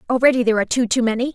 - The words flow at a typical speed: No, fast, 270 wpm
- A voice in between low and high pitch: No, high, 240 Hz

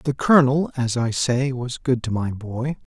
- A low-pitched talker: Yes, low, 130 Hz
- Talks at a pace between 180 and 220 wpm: Yes, fast, 205 wpm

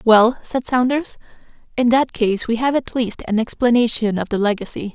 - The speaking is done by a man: No, female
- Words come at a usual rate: Yes, average, 180 wpm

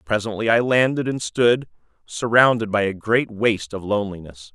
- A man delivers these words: Yes, male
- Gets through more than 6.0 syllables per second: No, 5.2 syllables/s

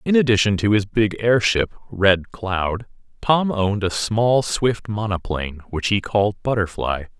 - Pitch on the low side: Yes, low, 105 Hz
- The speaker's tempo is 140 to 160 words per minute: Yes, average, 150 wpm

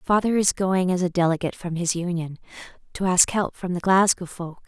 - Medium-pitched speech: Yes, medium, 180 Hz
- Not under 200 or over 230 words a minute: Yes, fast, 205 wpm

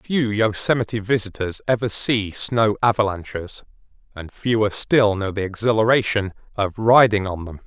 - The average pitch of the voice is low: Yes, low, 105 Hz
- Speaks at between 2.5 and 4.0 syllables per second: No, 4.7 syllables/s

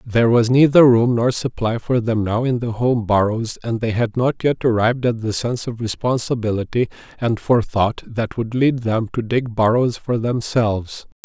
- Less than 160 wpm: No, average, 185 wpm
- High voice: No, low, 115 Hz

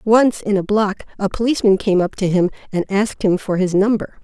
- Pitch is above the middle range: Yes, high, 200 Hz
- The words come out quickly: Yes, fast, 225 wpm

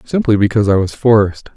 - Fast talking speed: No, average, 190 wpm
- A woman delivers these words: No, male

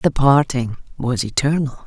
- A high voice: No, low, 130 Hz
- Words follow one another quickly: No, slow, 130 wpm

